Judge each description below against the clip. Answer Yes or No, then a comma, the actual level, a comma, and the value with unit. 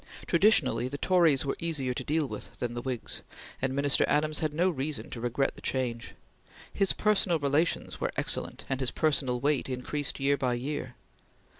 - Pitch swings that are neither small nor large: Yes, average, 3.4 semitones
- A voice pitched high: No, medium, 140 Hz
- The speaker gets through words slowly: No, average, 175 wpm